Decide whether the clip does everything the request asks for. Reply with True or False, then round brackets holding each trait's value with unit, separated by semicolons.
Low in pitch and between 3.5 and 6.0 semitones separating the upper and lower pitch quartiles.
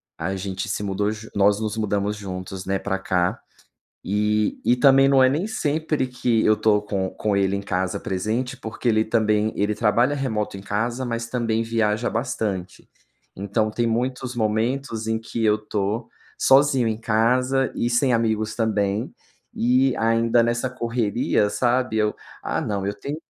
False (110 Hz; 2.9 semitones)